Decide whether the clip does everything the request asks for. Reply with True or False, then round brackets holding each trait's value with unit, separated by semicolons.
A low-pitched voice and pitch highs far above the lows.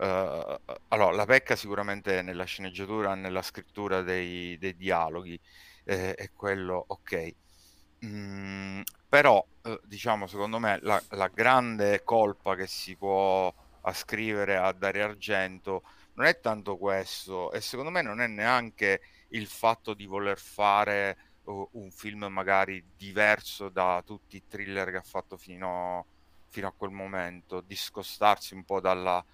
False (95 Hz; 1.7 semitones)